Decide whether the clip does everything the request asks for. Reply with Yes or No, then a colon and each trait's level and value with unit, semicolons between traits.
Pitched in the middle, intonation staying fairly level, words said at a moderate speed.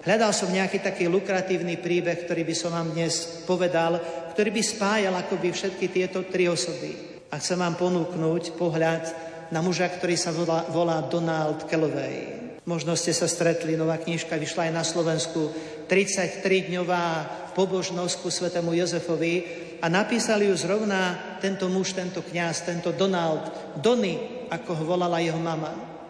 Yes: medium, 170 Hz; narrow, 1.8 semitones; average, 145 wpm